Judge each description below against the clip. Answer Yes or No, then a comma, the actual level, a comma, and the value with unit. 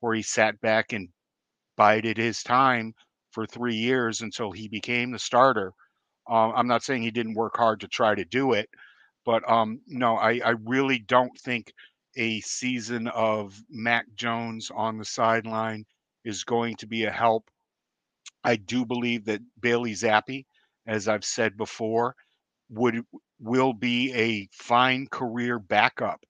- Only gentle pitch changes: Yes, narrow, 1.6 semitones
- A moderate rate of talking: Yes, average, 155 wpm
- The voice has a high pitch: No, low, 115 Hz